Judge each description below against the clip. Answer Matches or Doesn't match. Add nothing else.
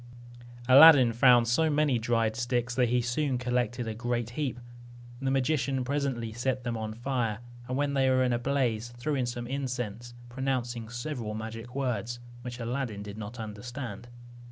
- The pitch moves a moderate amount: Doesn't match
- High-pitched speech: Doesn't match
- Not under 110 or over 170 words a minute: Matches